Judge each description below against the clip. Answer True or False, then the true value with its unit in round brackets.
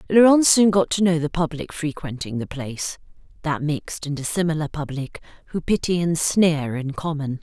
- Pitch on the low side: False (160 Hz)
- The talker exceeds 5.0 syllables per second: True (5.2 syllables/s)